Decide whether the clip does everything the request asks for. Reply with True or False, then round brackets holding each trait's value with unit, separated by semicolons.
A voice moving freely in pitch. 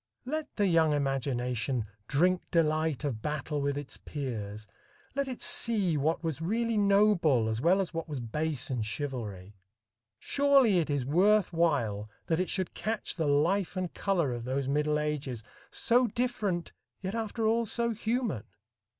True (7.1 semitones)